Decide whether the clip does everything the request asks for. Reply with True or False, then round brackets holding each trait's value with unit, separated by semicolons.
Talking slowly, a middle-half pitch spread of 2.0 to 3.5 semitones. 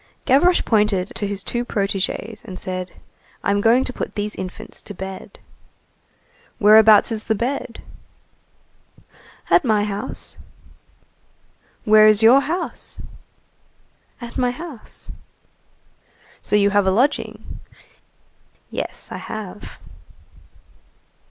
True (105 wpm; 3.1 semitones)